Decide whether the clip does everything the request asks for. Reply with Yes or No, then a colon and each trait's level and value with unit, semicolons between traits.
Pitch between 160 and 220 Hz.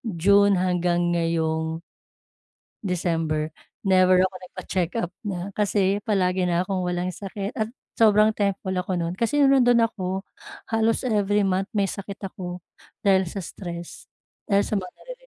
Yes: high, 190 Hz